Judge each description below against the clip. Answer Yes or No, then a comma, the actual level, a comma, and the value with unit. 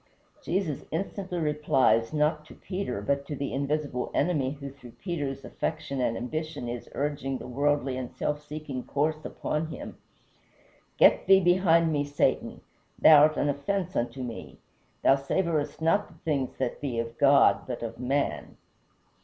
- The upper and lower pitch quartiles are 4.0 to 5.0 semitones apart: No, average, 3.0 semitones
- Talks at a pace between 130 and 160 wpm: Yes, average, 155 wpm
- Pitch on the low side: No, medium, 145 Hz